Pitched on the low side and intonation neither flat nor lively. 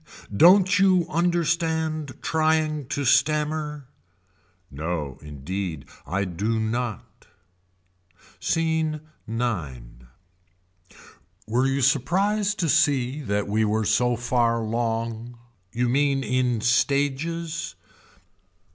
No: low, 130 Hz; wide, 6.1 semitones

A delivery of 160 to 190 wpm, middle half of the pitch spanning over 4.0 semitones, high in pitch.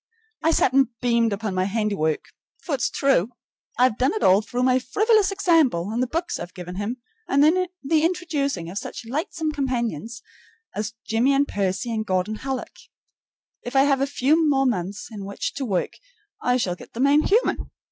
Yes: average, 185 wpm; wide, 5.5 semitones; very high, 250 Hz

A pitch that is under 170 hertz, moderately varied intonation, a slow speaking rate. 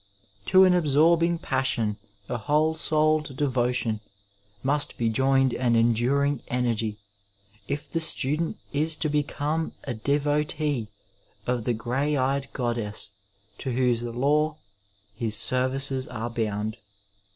Yes: low, 135 Hz; average, 4.0 semitones; slow, 120 wpm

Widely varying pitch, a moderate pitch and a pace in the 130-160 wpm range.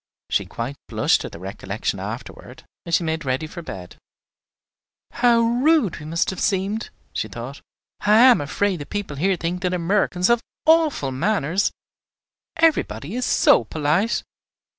Yes: wide, 7.0 semitones; medium, 180 Hz; average, 150 wpm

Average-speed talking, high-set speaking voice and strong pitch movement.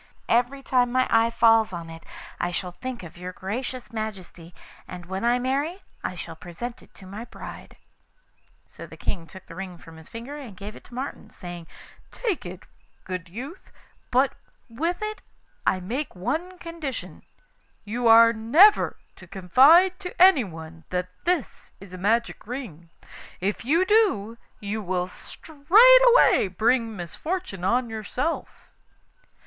Yes: average, 150 wpm; high, 230 Hz; wide, 7.2 semitones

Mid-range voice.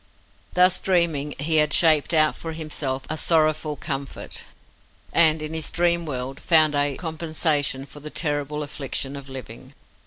Yes: medium, 155 Hz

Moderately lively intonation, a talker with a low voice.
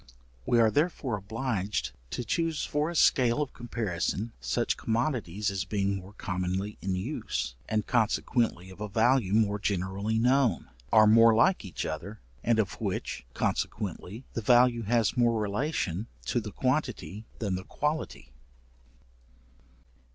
Yes: average, 3.8 semitones; low, 110 Hz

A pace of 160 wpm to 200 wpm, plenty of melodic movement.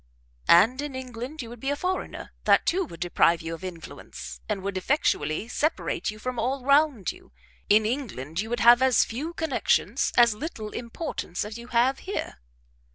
Yes: average, 180 wpm; wide, 5.7 semitones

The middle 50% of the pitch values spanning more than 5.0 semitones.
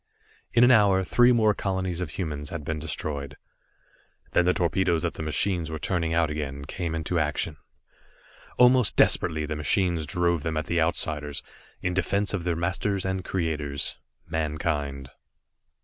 No: average, 3.6 semitones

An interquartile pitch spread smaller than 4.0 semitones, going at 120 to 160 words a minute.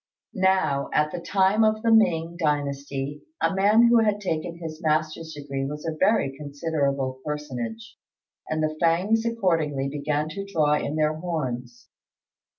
No: average, 4.8 semitones; average, 150 wpm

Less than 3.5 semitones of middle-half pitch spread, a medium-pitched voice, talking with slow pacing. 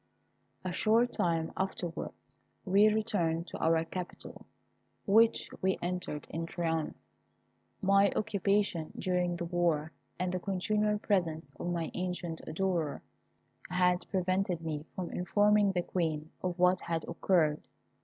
Yes: average, 2.8 semitones; medium, 180 Hz; slow, 125 wpm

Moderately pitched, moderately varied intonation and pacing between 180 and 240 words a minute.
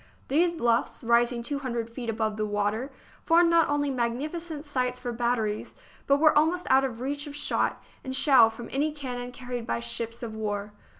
No: very high, 250 Hz; average, 4.0 semitones; average, 190 wpm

